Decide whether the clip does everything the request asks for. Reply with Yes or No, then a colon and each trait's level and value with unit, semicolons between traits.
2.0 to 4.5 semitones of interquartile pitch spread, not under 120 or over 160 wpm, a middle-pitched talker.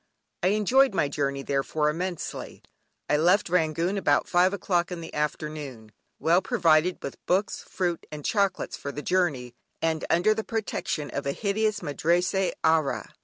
Yes: average, 4.2 semitones; average, 155 wpm; medium, 170 Hz